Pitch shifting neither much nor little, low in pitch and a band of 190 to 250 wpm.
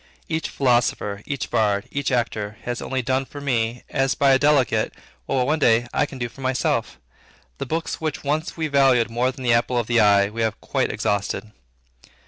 Yes: average, 3.6 semitones; low, 125 Hz; average, 195 wpm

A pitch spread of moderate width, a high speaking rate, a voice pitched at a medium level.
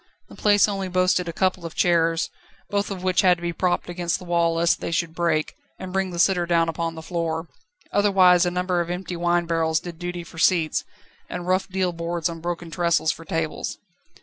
No: narrow, 1.5 semitones; fast, 215 wpm; medium, 175 Hz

